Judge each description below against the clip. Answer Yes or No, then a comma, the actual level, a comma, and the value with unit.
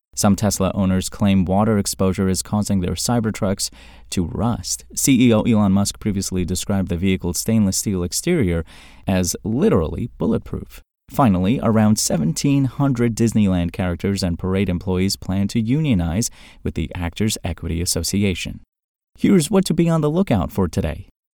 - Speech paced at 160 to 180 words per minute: No, average, 145 wpm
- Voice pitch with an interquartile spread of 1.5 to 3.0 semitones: No, average, 3.6 semitones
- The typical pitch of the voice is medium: No, very low, 95 Hz